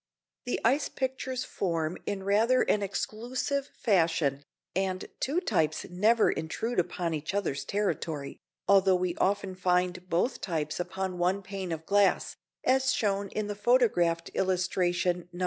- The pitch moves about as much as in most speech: Yes, average, 3.3 semitones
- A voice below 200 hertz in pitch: Yes, high, 190 Hz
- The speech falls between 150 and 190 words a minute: No, average, 140 wpm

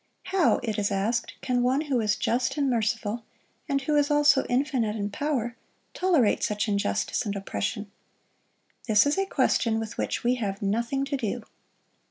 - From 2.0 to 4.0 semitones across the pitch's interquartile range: No, average, 4.7 semitones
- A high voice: Yes, high, 235 Hz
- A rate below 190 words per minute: Yes, average, 170 wpm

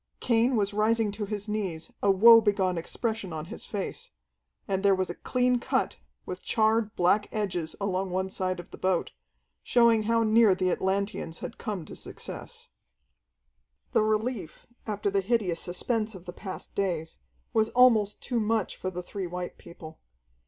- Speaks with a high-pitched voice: Yes, high, 200 Hz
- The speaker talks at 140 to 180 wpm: Yes, average, 165 wpm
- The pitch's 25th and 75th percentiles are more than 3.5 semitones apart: No, average, 3.2 semitones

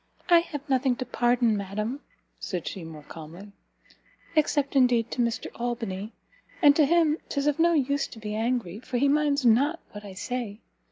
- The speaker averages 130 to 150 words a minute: No, average, 175 wpm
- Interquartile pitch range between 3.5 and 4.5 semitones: No, average, 5.1 semitones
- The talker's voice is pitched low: No, high, 245 Hz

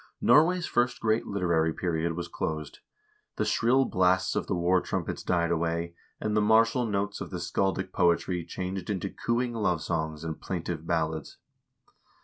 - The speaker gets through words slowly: No, average, 155 wpm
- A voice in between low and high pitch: No, very low, 90 Hz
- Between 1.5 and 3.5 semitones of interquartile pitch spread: No, average, 4.2 semitones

